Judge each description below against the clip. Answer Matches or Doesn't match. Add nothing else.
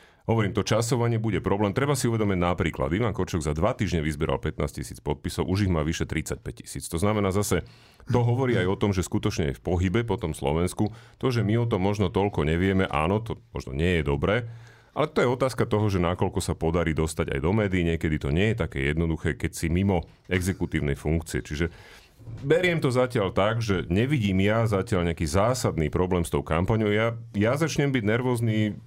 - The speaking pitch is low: Matches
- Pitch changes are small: Doesn't match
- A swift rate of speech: Matches